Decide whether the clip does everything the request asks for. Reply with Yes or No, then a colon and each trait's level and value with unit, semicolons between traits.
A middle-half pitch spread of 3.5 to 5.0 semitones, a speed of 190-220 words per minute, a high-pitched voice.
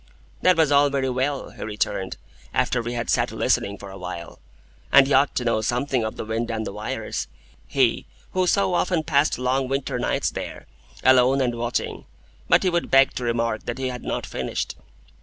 No: average, 3.8 semitones; average, 195 wpm; low, 125 Hz